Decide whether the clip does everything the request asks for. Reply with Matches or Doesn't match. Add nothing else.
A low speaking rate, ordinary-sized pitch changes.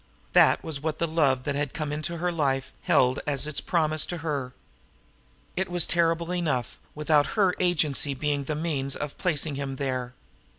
Doesn't match